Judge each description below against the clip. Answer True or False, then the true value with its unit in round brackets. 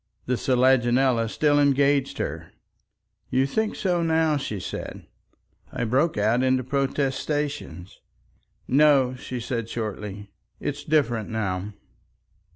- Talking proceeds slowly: True (110 wpm)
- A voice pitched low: True (130 Hz)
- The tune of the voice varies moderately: True (4.0 semitones)